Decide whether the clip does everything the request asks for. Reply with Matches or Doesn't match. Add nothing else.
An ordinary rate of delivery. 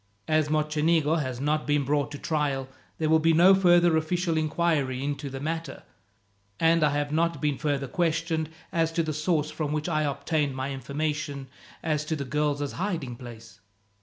Matches